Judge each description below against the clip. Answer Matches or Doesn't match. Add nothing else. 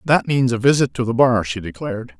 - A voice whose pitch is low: Matches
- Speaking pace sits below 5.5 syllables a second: Doesn't match